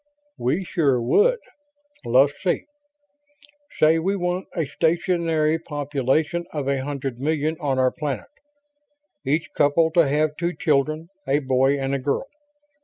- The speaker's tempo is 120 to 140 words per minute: Yes, slow, 135 wpm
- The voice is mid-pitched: Yes, medium, 150 Hz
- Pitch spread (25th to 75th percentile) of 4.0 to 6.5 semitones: No, average, 3.2 semitones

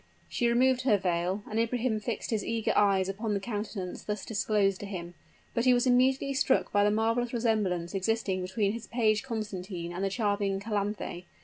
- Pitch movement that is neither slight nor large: Yes, average, 3.0 semitones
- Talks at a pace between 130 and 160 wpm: No, average, 185 wpm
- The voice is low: No, high, 210 Hz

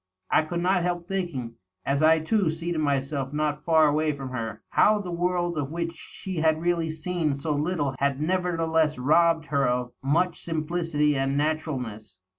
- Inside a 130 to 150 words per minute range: No, average, 170 wpm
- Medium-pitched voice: Yes, medium, 155 Hz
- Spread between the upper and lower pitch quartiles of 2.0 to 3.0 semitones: No, average, 3.5 semitones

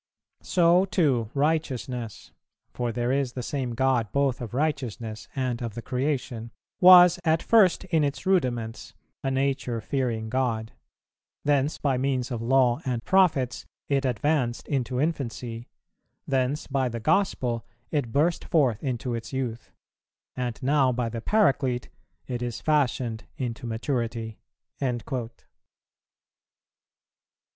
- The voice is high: No, low, 130 Hz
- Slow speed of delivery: Yes, slow, 125 wpm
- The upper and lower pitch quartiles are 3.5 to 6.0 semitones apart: No, average, 3.1 semitones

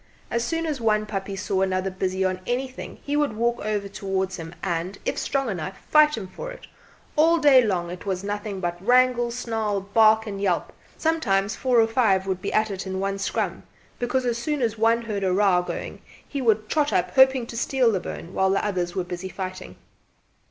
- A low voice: No, high, 210 Hz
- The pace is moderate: No, fast, 210 wpm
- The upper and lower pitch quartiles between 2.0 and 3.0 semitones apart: No, average, 4.3 semitones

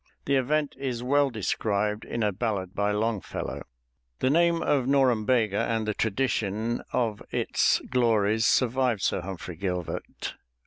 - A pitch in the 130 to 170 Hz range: No, low, 115 Hz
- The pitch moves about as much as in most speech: Yes, average, 3.9 semitones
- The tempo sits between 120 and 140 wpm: Yes, slow, 135 wpm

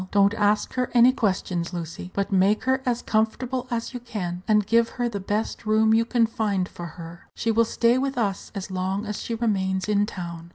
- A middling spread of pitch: Yes, average, 3.5 semitones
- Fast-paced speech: Yes, fast, 210 wpm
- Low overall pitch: No, high, 210 Hz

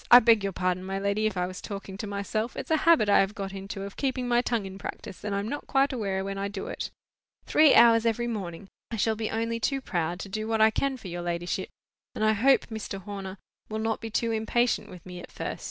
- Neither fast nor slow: No, fast, 255 wpm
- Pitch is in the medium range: No, high, 210 Hz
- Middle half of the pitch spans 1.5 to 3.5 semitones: Yes, average, 3.0 semitones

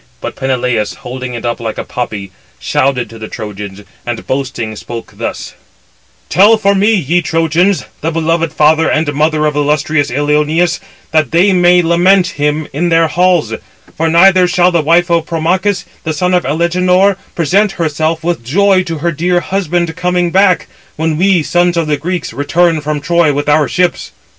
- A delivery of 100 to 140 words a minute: No, average, 175 wpm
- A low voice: No, medium, 165 Hz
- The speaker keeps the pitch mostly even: No, average, 3.4 semitones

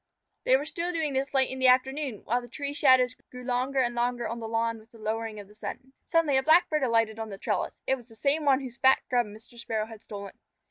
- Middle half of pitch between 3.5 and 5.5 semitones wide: No, average, 3.1 semitones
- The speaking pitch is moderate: No, very high, 250 Hz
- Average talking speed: No, fast, 250 wpm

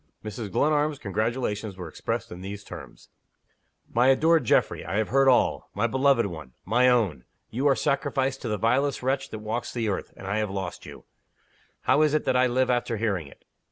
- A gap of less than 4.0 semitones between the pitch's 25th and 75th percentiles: No, average, 4.6 semitones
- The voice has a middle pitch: No, low, 120 Hz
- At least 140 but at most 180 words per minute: No, average, 195 wpm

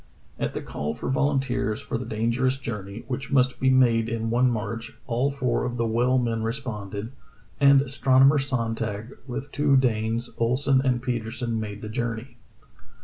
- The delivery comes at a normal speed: Yes, average, 160 wpm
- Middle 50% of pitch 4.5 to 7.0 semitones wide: No, average, 2.7 semitones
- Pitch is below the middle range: Yes, low, 120 Hz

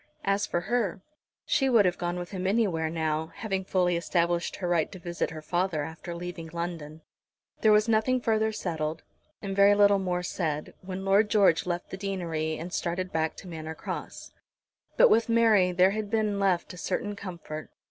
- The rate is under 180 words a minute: No, average, 185 wpm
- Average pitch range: Yes, average, 3.2 semitones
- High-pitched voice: No, medium, 180 Hz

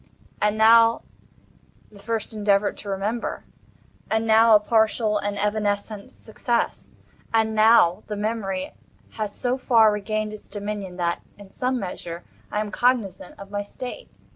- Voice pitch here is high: Yes, high, 210 Hz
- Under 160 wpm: Yes, average, 140 wpm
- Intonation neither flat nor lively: No, narrow, 1.8 semitones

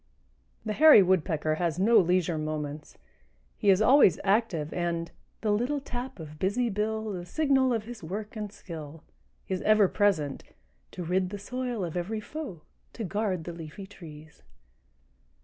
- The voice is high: Yes, high, 195 Hz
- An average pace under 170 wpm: Yes, average, 155 wpm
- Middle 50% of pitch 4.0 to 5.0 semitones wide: Yes, average, 4.7 semitones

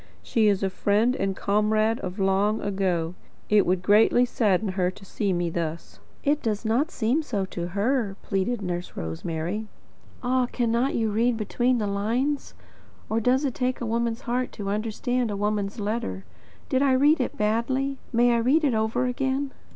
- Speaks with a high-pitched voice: Yes, high, 220 Hz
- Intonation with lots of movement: No, average, 4.0 semitones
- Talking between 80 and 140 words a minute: No, average, 175 wpm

